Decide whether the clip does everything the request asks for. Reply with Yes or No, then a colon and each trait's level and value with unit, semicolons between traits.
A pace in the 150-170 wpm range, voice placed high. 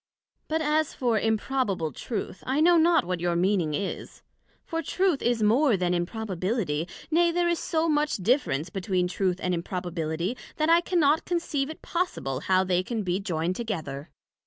Yes: average, 165 wpm; high, 210 Hz